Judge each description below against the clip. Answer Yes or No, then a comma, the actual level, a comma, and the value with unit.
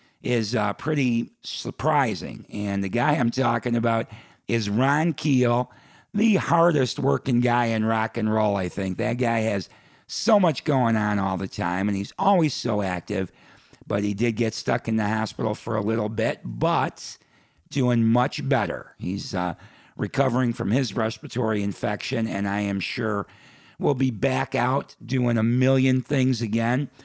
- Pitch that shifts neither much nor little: Yes, average, 3.8 semitones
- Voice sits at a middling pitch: No, low, 115 Hz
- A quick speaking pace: No, average, 165 wpm